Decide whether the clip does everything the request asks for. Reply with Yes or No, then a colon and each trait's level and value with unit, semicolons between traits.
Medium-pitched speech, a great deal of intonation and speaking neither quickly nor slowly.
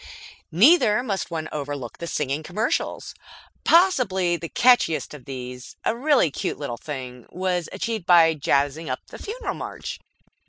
Yes: medium, 170 Hz; wide, 7.6 semitones; average, 145 wpm